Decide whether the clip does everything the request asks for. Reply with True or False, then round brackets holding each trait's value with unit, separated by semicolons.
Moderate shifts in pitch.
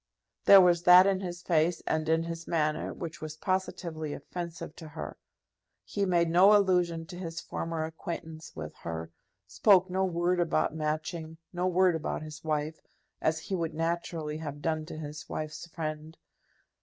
False (2.2 semitones)